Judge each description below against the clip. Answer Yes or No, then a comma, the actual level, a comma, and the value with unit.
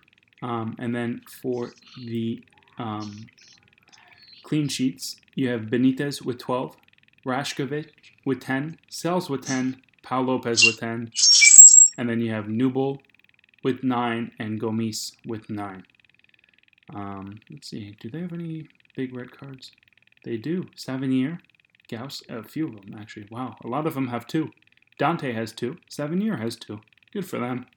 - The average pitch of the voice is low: Yes, low, 125 Hz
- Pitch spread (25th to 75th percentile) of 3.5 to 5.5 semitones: No, average, 3.0 semitones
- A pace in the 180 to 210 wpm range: No, average, 150 wpm